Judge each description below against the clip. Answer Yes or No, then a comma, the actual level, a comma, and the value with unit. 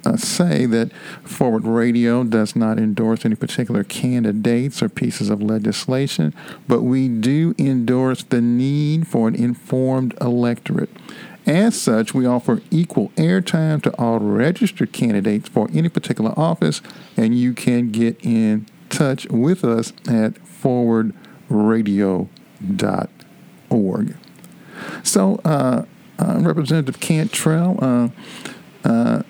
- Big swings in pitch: Yes, wide, 6.4 semitones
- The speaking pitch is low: Yes, low, 125 Hz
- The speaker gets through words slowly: Yes, slow, 115 wpm